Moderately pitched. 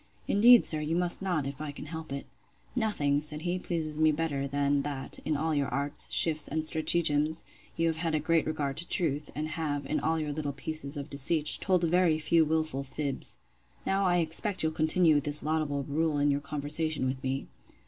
Yes: medium, 155 Hz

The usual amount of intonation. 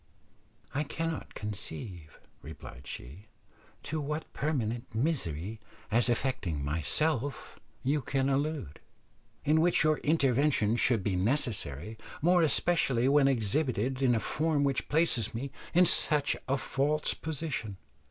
No: wide, 6.0 semitones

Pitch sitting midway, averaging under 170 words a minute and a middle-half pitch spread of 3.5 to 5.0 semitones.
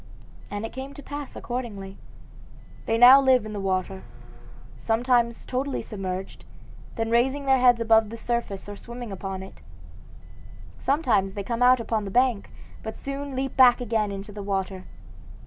No: high, 230 Hz; average, 160 wpm; average, 4.1 semitones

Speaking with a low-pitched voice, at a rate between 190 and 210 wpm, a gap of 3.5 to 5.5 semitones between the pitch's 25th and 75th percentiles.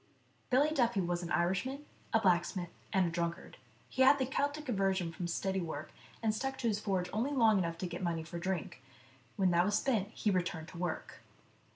No: high, 190 Hz; average, 200 wpm; average, 5.0 semitones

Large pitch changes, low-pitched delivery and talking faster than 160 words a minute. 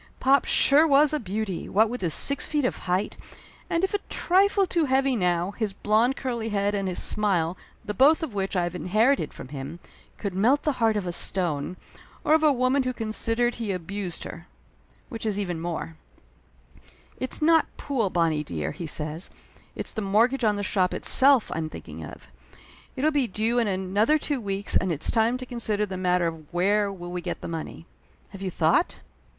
No: wide, 6.0 semitones; high, 210 Hz; average, 200 wpm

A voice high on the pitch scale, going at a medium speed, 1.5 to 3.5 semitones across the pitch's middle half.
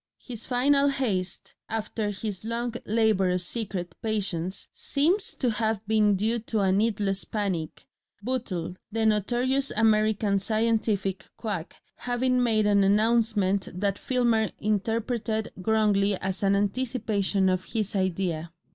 No: high, 215 Hz; slow, 120 wpm; average, 2.9 semitones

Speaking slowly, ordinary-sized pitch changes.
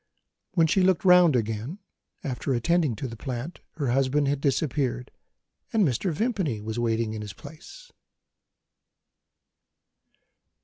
No: slow, 125 wpm; wide, 6.2 semitones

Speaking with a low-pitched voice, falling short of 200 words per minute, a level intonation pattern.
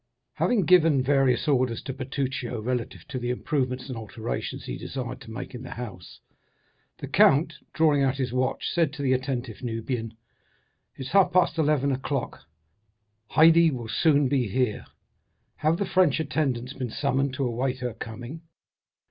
No: low, 130 Hz; average, 160 wpm; average, 3.1 semitones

